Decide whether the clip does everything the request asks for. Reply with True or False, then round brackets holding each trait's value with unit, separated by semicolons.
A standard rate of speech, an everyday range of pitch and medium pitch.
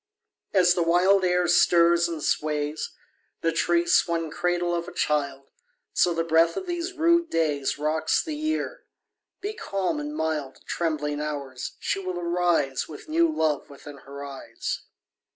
True (160 wpm; 3.4 semitones; 170 Hz)